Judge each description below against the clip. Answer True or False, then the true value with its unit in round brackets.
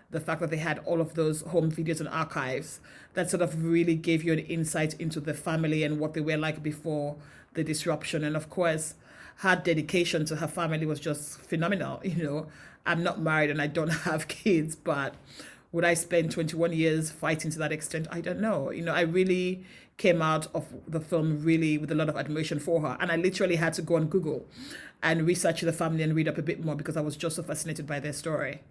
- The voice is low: False (160 Hz)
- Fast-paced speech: True (230 wpm)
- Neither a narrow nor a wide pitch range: False (1.5 semitones)